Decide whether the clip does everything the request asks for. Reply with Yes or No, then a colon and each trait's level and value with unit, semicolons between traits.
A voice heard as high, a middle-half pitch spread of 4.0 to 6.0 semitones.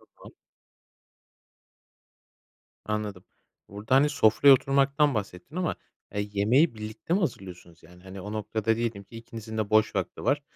No: low, 110 Hz; average, 4.7 semitones